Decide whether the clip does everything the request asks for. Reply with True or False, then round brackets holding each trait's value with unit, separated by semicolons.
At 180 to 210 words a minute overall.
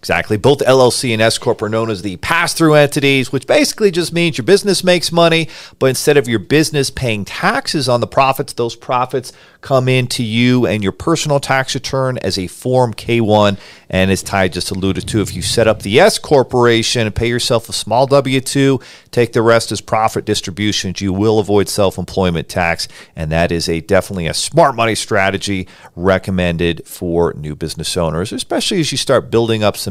True (195 wpm)